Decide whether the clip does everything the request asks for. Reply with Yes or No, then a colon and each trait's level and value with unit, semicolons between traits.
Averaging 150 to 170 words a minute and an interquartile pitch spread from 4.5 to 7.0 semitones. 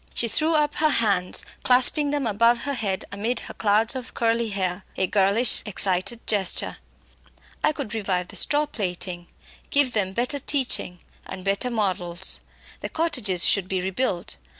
Yes: average, 155 wpm; average, 5.1 semitones